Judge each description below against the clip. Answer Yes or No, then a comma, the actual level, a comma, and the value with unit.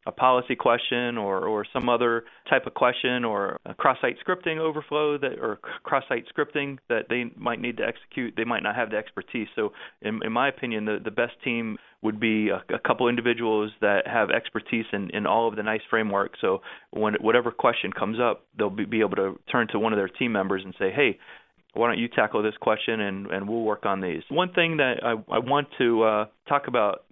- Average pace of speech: No, fast, 220 wpm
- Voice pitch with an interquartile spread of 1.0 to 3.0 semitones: Yes, narrow, 2.4 semitones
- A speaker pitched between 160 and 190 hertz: No, low, 115 Hz